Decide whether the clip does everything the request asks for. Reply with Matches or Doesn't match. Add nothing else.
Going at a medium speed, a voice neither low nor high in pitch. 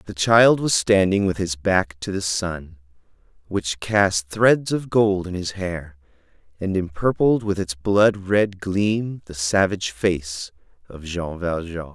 Doesn't match